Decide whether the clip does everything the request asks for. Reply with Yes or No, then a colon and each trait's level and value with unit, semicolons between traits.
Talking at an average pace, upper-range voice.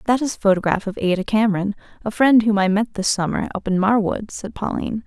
No: fast, 225 wpm; high, 210 Hz